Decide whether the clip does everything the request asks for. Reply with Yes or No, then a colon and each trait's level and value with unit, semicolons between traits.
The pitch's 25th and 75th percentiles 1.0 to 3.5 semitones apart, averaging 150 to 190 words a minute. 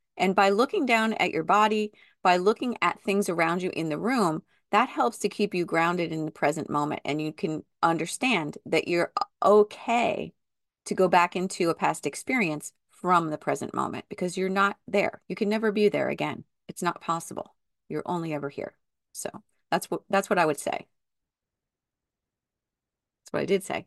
No: average, 4.0 semitones; average, 185 wpm